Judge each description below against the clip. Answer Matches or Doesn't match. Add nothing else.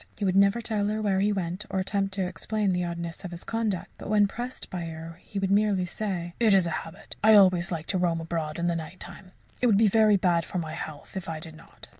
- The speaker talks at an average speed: Doesn't match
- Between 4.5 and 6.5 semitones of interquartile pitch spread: Doesn't match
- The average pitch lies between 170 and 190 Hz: Matches